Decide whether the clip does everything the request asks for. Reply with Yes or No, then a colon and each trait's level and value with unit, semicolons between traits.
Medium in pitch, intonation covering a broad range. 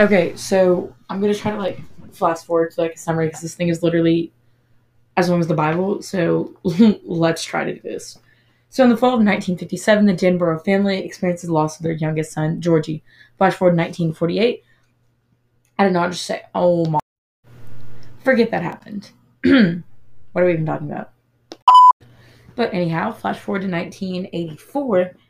No: medium, 175 Hz; average, 3.2 semitones